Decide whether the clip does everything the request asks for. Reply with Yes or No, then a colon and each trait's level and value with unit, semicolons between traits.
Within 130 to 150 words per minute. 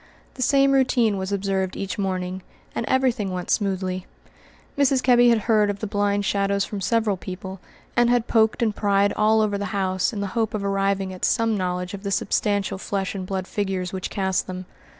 No: average, 200 wpm